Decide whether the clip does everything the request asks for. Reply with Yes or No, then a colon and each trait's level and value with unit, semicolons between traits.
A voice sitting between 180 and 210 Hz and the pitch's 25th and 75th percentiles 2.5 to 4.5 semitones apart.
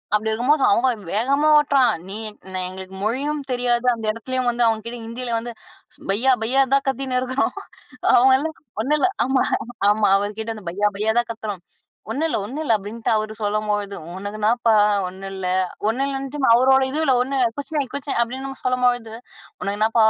No: high, 240 Hz; average, 3.9 semitones